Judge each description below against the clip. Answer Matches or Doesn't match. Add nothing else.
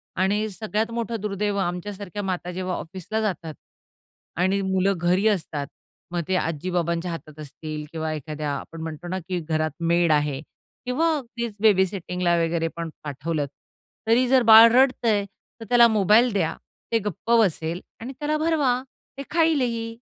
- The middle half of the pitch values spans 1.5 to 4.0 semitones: Doesn't match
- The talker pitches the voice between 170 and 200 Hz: Matches